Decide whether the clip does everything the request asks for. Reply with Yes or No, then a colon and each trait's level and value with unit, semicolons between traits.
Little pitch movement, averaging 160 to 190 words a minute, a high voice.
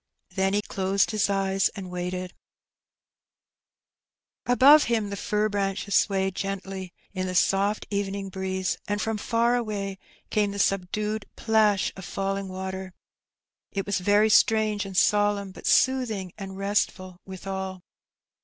No: narrow, 1.6 semitones; slow, 135 wpm; high, 195 Hz